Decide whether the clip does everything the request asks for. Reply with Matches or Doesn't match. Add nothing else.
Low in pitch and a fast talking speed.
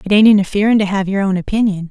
Doesn't match